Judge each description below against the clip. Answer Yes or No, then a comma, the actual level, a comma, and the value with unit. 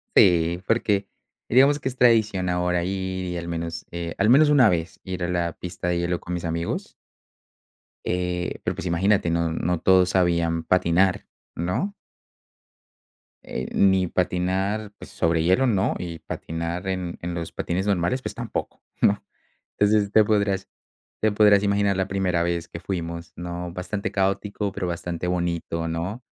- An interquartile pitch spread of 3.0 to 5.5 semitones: No, narrow, 2.6 semitones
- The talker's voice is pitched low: Yes, very low, 90 Hz